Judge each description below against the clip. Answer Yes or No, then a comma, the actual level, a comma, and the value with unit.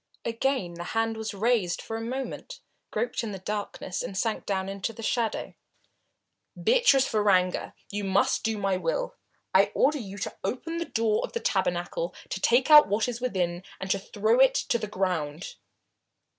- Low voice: No, high, 220 Hz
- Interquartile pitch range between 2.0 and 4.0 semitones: No, average, 4.5 semitones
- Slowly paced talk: No, average, 175 wpm